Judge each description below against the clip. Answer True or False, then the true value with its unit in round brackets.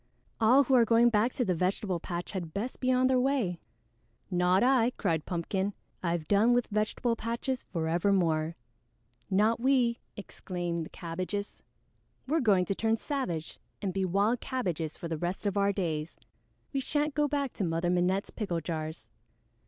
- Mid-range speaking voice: False (200 Hz)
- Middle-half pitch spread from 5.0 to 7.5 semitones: True (5.6 semitones)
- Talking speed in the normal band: True (165 wpm)